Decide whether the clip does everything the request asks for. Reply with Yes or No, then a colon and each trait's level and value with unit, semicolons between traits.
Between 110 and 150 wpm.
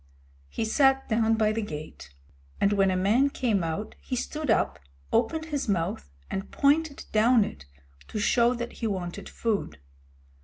No: average, 160 wpm